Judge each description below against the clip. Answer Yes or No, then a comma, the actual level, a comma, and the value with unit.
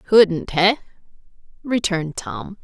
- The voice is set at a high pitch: No, medium, 180 Hz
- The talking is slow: Yes, slow, 90 wpm